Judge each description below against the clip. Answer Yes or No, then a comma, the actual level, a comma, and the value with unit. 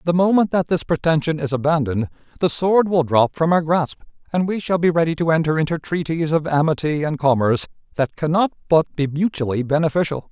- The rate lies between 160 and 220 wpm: Yes, average, 200 wpm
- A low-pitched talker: No, medium, 160 Hz